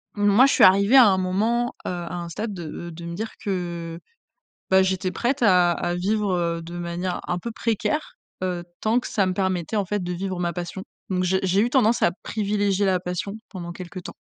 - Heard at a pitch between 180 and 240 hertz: Yes, medium, 185 Hz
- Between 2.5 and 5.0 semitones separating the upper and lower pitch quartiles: Yes, average, 3.0 semitones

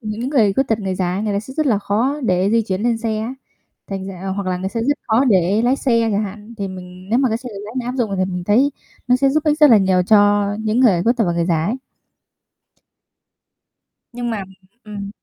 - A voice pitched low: No, high, 215 Hz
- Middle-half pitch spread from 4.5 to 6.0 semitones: No, average, 3.8 semitones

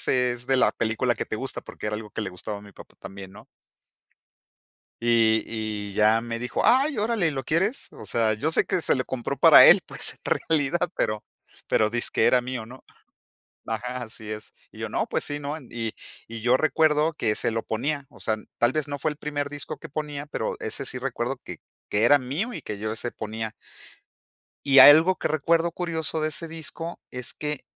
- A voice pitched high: No, low, 130 Hz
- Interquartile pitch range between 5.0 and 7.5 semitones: Yes, wide, 5.5 semitones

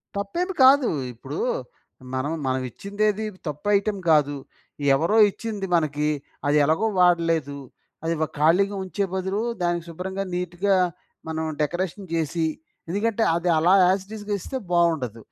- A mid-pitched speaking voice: Yes, medium, 175 Hz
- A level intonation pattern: No, average, 4.1 semitones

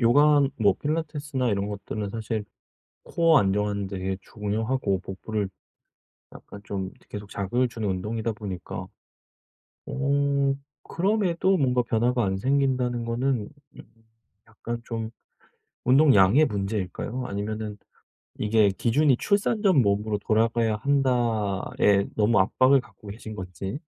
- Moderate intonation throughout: Yes, average, 4.7 semitones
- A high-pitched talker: No, low, 115 Hz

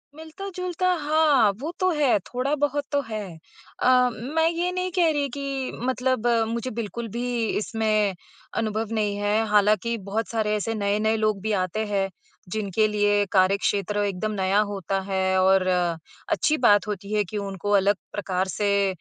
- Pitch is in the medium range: No, high, 215 Hz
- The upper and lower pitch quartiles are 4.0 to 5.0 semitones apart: Yes, average, 4.4 semitones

